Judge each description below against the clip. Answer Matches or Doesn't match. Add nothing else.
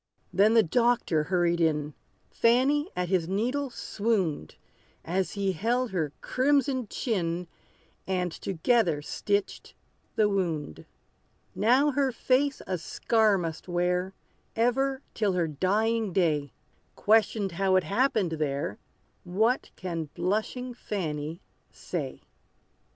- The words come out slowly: Matches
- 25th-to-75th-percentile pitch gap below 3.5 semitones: Doesn't match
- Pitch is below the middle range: Doesn't match